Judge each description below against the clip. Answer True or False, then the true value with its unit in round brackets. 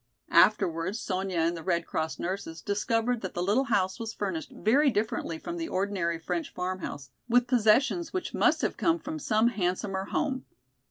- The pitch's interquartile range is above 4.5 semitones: True (5.2 semitones)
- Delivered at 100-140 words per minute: False (170 wpm)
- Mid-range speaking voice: False (200 Hz)